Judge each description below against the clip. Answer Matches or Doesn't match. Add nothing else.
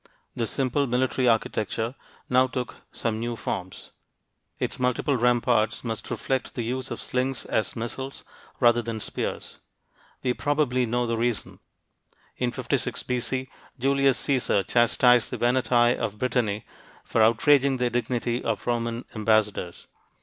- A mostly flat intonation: Matches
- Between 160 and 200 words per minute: Doesn't match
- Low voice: Matches